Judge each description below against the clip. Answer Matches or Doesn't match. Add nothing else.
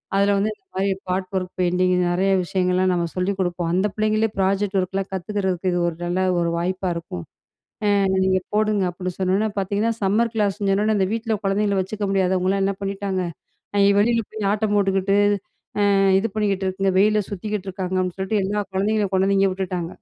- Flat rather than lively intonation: Matches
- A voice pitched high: Matches